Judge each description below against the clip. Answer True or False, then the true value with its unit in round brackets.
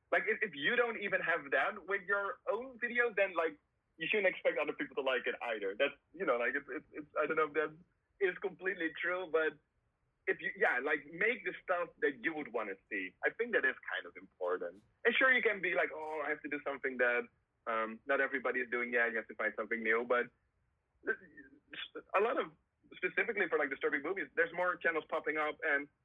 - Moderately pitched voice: True (165 Hz)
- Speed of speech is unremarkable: False (225 wpm)